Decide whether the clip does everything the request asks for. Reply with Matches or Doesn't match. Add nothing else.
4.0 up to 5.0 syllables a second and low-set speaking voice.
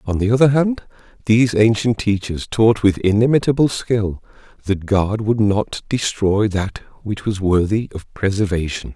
Matches